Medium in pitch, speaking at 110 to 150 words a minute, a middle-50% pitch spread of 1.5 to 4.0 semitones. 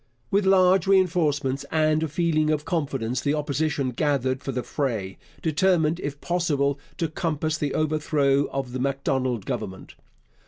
Yes: medium, 150 Hz; average, 145 wpm; average, 3.0 semitones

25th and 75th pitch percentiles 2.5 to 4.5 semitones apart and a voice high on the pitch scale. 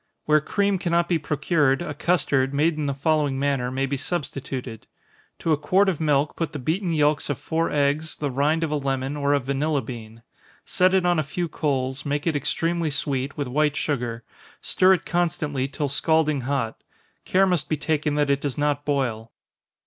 No: average, 2.8 semitones; medium, 145 Hz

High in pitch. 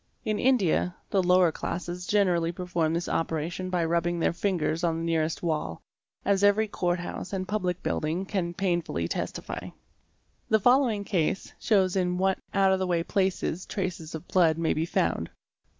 No: medium, 180 Hz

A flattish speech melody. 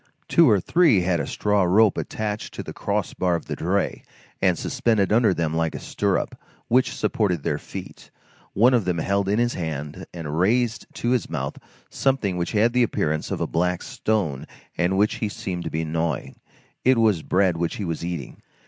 No: average, 4.7 semitones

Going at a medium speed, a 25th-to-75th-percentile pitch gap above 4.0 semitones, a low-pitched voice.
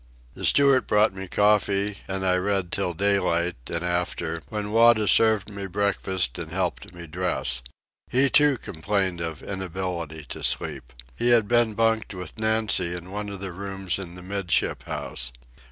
No: average, 165 wpm; average, 3.1 semitones; very low, 95 Hz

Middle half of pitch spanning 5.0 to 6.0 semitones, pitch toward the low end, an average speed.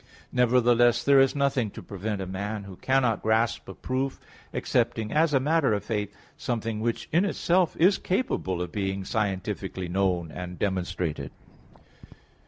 Yes: wide, 5.5 semitones; low, 110 Hz; average, 150 wpm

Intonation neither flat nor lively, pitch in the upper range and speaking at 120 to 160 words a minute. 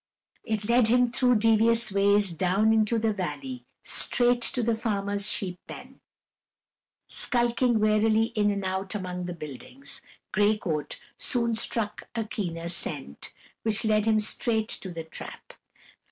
Yes: average, 3.1 semitones; high, 215 Hz; average, 140 wpm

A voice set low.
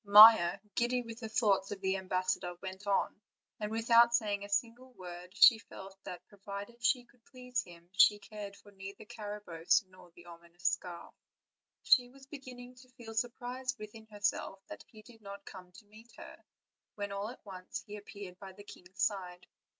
No: high, 205 Hz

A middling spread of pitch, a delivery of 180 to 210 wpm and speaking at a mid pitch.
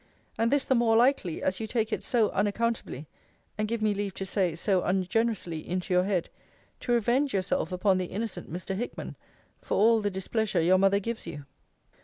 No: average, 3.7 semitones; average, 190 wpm; high, 205 Hz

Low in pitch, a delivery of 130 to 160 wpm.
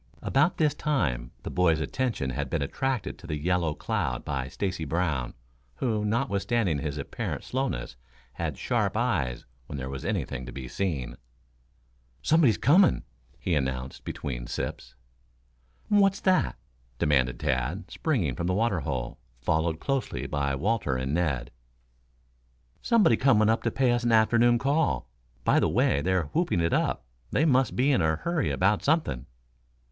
Yes: very low, 90 Hz; average, 150 wpm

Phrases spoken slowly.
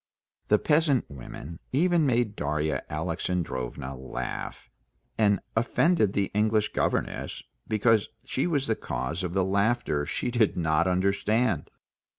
Yes: slow, 125 wpm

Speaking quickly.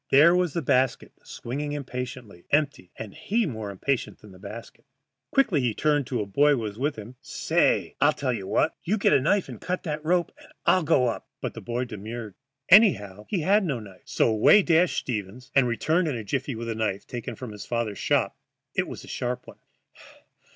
Yes: fast, 210 wpm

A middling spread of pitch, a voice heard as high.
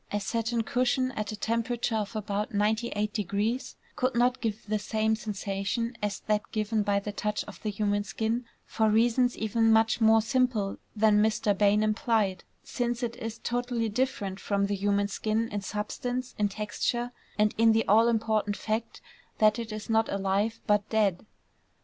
No: narrow, 1.9 semitones; high, 215 Hz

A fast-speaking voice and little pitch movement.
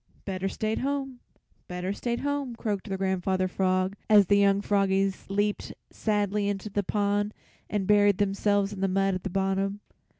No: average, 165 wpm; narrow, 1.3 semitones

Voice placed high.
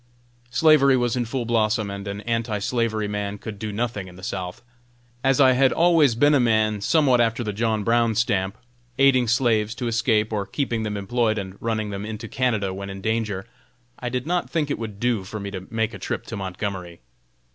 No: low, 110 Hz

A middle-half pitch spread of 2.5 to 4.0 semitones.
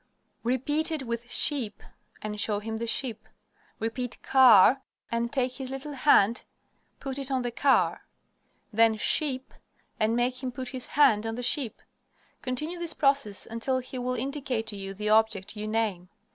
Yes: average, 3.3 semitones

